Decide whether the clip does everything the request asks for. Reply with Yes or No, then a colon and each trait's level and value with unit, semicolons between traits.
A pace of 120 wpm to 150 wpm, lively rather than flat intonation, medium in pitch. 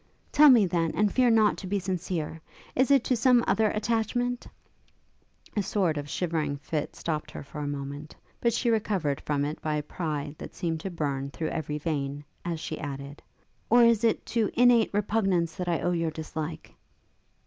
No: average, 190 wpm; wide, 6.5 semitones; medium, 170 Hz